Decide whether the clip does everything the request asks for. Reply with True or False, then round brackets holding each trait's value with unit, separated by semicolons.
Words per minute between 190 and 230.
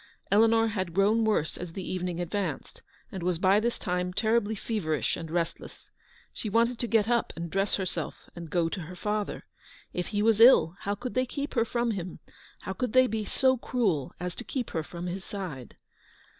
True (200 wpm)